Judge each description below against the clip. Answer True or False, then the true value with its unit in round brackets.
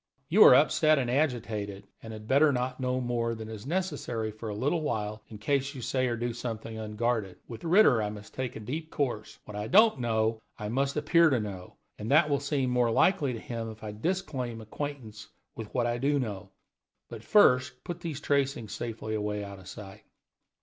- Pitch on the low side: True (120 Hz)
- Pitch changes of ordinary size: True (4.4 semitones)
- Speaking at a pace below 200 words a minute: False (205 wpm)